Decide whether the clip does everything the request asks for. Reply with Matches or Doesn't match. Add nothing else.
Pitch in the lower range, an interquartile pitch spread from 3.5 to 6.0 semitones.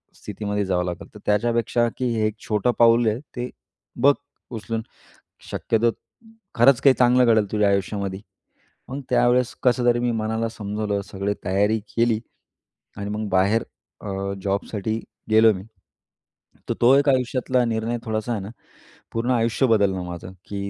Doesn't match